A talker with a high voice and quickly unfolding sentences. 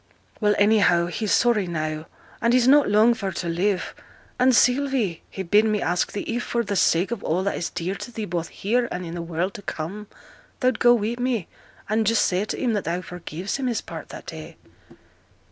Yes: high, 205 Hz; fast, 215 wpm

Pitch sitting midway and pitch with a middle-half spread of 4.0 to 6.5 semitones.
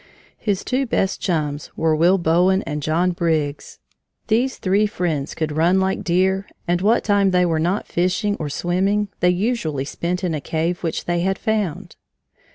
No: medium, 180 Hz; average, 3.2 semitones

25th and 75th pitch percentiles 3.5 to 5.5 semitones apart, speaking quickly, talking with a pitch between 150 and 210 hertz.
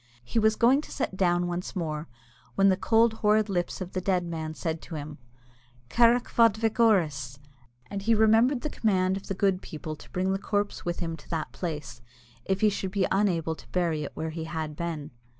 Yes: average, 4.7 semitones; fast, 210 wpm; medium, 185 Hz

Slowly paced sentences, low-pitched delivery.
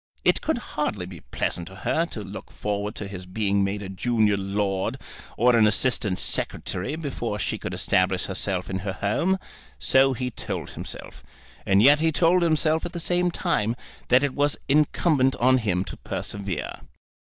No: average, 175 wpm; low, 110 Hz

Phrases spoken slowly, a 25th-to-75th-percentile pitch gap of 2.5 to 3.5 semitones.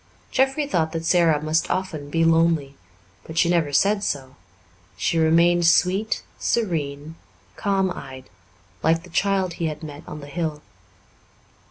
No: average, 145 wpm; average, 3.1 semitones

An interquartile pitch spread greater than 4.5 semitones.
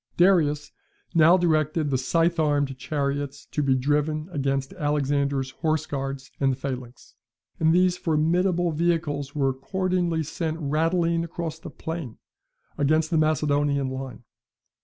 No: average, 3.1 semitones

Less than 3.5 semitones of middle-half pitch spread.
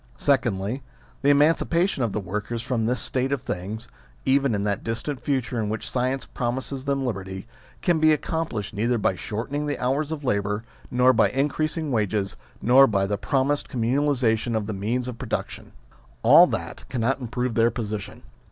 No: average, 4.3 semitones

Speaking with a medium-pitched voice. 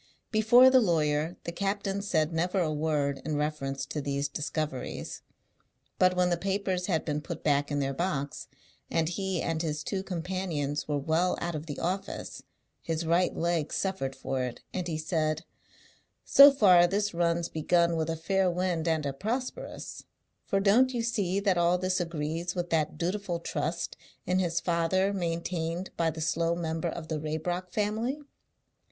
Yes: medium, 170 Hz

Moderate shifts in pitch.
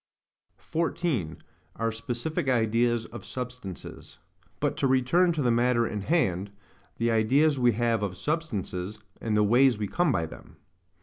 Yes: average, 4.3 semitones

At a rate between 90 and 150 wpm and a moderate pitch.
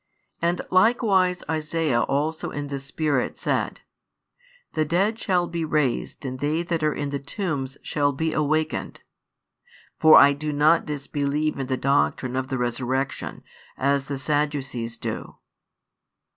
Yes: average, 145 wpm; medium, 145 Hz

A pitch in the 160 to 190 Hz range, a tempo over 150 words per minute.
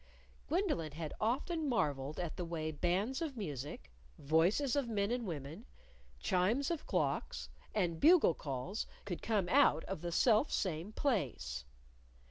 No: medium, 185 Hz; average, 140 wpm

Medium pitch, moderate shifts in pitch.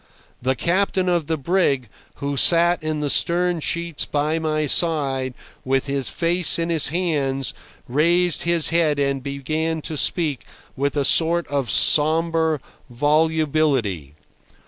Yes: medium, 155 Hz; average, 3.4 semitones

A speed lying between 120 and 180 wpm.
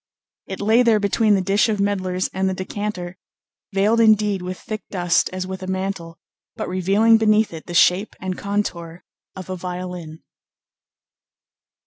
Yes: average, 155 wpm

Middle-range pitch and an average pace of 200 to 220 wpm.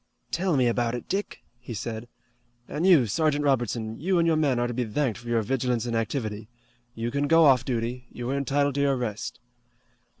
No: low, 125 Hz; fast, 205 wpm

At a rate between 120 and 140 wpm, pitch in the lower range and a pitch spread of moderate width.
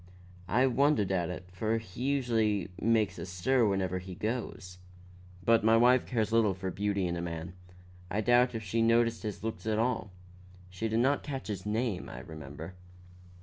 No: average, 180 wpm; low, 110 Hz; average, 4.0 semitones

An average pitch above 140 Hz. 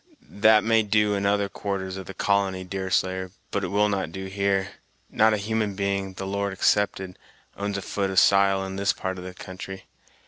No: low, 100 Hz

